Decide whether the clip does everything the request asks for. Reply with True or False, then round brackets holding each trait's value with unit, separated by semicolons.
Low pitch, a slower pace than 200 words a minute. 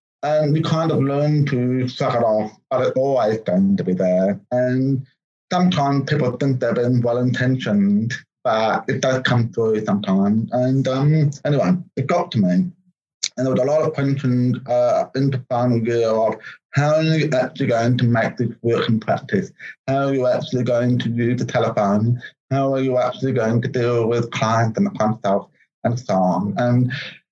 True (125 Hz; 185 wpm)